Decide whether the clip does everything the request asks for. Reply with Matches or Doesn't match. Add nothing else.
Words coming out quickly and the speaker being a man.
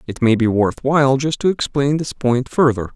Matches